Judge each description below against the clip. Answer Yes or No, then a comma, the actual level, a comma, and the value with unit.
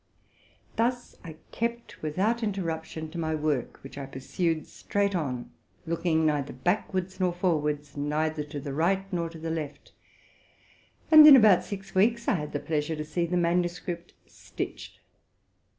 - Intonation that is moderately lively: Yes, average, 3.9 semitones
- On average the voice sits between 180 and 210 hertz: No, medium, 165 Hz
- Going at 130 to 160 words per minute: Yes, average, 155 wpm